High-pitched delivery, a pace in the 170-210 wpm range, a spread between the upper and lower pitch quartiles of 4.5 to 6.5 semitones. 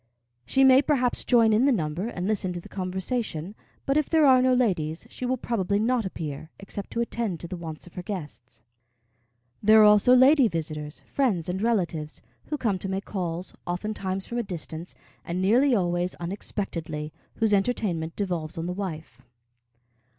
Yes: high, 195 Hz; average, 175 wpm; wide, 5.6 semitones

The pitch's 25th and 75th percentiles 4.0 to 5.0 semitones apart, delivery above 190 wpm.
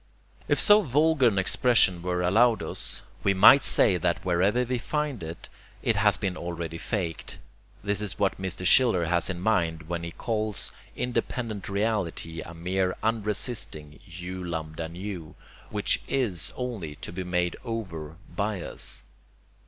No: average, 4.7 semitones; average, 150 wpm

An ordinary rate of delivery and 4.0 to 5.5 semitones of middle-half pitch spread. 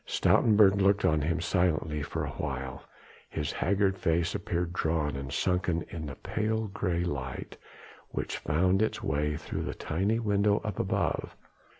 Yes: average, 150 wpm; average, 4.7 semitones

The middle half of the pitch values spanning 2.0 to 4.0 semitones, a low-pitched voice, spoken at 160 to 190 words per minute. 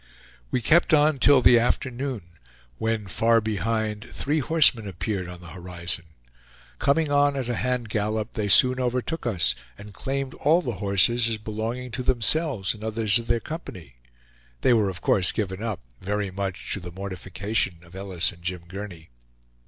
No: average, 4.8 semitones; low, 110 Hz; average, 170 wpm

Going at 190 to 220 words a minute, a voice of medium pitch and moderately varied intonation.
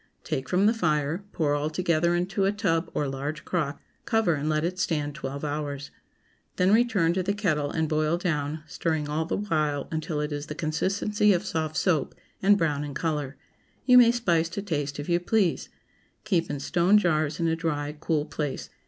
Yes: average, 195 wpm; medium, 160 Hz; average, 3.6 semitones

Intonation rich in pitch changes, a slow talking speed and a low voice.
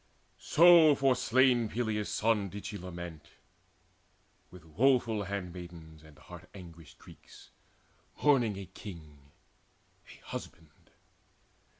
Yes: wide, 6.1 semitones; slow, 100 wpm; low, 100 Hz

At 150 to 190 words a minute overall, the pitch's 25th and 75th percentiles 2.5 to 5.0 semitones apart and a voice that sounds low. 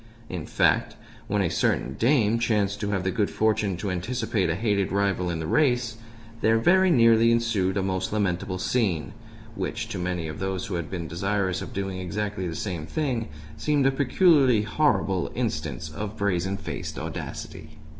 Yes: average, 175 wpm; average, 3.9 semitones; low, 100 Hz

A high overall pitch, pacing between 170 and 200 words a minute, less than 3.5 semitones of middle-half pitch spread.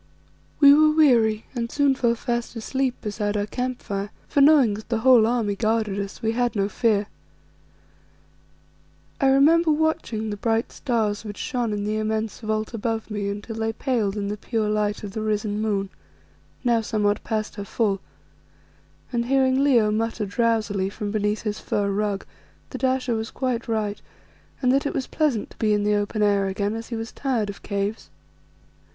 Yes: high, 220 Hz; average, 180 wpm; average, 2.9 semitones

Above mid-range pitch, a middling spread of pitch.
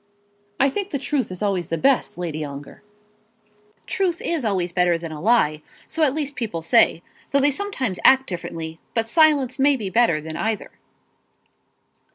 No: high, 225 Hz; wide, 8.6 semitones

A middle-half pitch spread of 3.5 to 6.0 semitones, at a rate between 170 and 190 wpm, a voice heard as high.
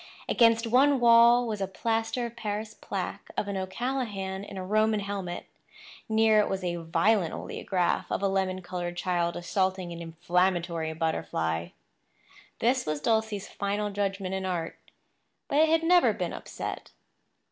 No: average, 4.0 semitones; average, 150 wpm; high, 195 Hz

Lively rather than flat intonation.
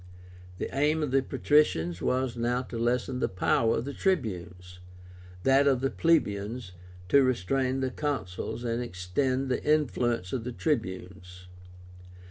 Yes: wide, 6.1 semitones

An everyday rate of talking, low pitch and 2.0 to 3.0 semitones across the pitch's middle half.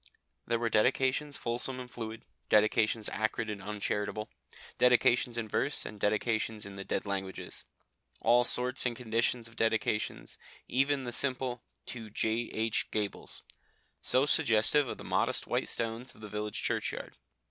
Yes: average, 145 wpm; low, 115 Hz; narrow, 2.6 semitones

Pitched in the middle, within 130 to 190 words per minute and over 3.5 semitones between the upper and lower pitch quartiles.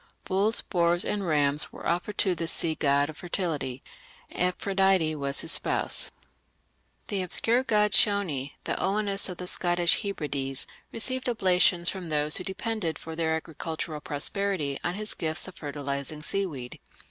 Yes: medium, 175 Hz; average, 145 wpm; average, 4.6 semitones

